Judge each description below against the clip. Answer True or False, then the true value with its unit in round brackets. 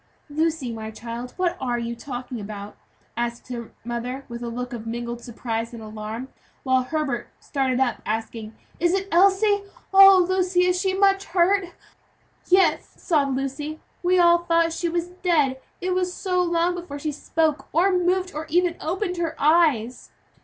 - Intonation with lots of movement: True (6.9 semitones)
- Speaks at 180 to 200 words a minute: False (165 wpm)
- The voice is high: True (310 Hz)